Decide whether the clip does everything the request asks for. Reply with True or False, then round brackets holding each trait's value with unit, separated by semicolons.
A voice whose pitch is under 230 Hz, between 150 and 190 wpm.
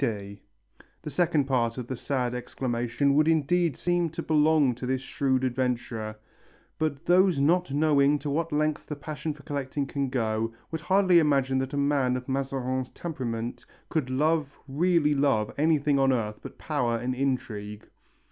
True (140 Hz; 165 wpm)